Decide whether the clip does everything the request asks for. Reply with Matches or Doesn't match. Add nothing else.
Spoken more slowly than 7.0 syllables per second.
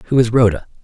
Doesn't match